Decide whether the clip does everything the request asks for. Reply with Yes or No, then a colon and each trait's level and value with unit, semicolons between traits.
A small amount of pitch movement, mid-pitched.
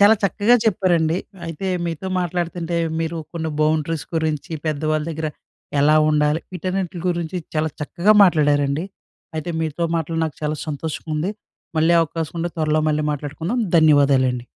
Yes: narrow, 2.2 semitones; medium, 160 Hz